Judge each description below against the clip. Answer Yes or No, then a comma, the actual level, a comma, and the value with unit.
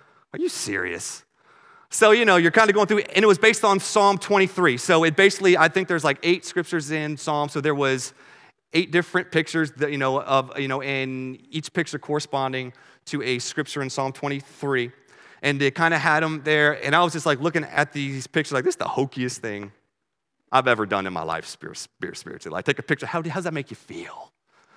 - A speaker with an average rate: No, fast, 225 wpm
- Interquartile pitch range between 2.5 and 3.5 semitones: No, average, 4.6 semitones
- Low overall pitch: No, medium, 150 Hz